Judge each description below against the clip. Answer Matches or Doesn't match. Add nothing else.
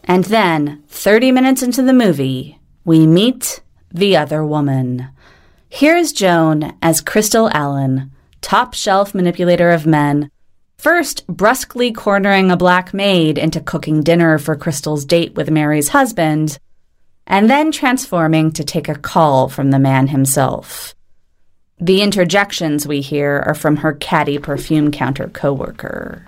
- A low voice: Doesn't match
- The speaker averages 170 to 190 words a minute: Doesn't match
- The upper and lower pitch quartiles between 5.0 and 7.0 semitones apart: Matches